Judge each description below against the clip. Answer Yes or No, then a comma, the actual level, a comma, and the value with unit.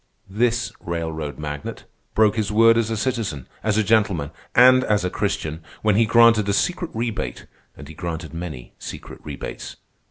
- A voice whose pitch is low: Yes, low, 105 Hz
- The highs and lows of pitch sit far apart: Yes, wide, 6.1 semitones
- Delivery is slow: No, average, 165 wpm